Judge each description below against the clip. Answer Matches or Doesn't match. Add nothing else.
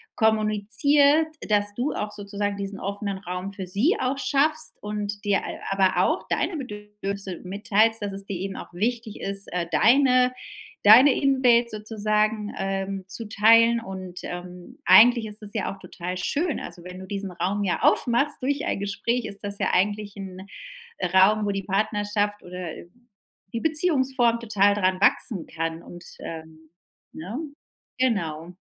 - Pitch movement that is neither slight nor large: Matches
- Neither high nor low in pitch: Doesn't match